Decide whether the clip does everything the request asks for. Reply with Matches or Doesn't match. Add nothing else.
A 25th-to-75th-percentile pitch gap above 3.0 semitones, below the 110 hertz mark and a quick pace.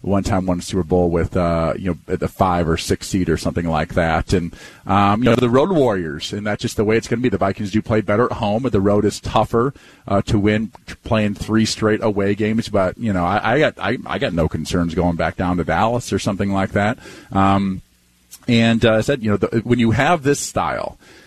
Matches